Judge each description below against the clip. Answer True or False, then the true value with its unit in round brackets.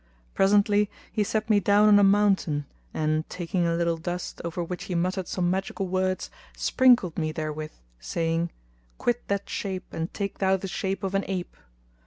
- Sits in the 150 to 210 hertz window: True (185 Hz)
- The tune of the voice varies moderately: True (3.0 semitones)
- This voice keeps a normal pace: True (175 wpm)